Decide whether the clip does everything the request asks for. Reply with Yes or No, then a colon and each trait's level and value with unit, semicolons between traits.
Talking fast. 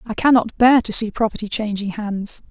No: average, 190 wpm